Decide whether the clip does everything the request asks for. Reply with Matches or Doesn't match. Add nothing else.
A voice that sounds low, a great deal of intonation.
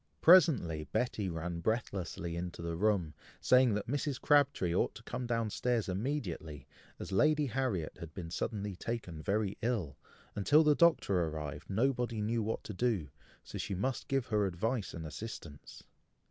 Matches